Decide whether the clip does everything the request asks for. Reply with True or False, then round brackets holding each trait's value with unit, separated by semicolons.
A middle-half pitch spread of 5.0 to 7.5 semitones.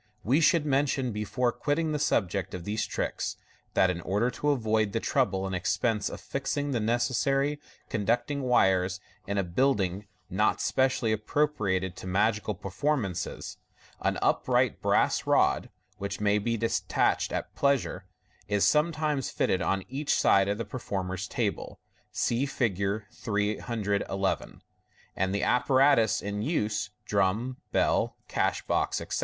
True (5.3 semitones)